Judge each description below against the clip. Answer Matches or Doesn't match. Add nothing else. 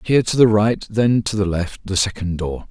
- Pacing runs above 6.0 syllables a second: Doesn't match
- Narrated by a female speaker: Doesn't match